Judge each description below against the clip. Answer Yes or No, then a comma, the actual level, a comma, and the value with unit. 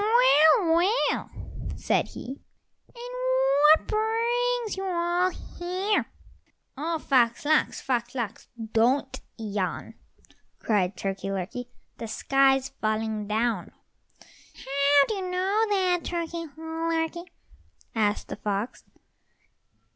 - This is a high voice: Yes, very high, 310 Hz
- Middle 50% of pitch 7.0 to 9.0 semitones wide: Yes, wide, 8.1 semitones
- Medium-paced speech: No, slow, 100 wpm